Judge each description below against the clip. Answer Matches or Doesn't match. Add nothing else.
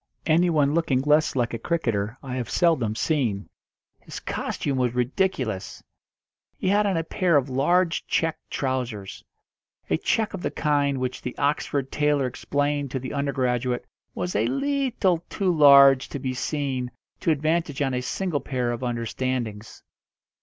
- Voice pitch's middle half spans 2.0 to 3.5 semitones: Doesn't match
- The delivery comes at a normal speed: Matches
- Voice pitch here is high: Doesn't match